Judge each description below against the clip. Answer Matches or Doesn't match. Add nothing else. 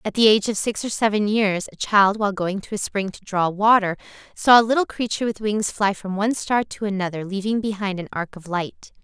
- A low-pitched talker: Doesn't match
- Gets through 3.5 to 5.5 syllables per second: Doesn't match